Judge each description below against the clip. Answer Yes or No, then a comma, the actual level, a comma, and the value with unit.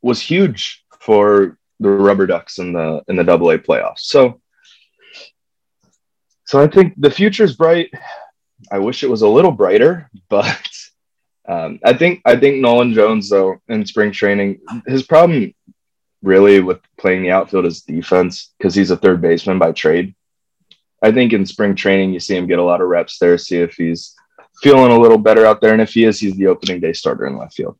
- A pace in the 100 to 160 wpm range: No, average, 195 wpm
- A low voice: Yes, low, 105 Hz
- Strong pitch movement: Yes, wide, 6.7 semitones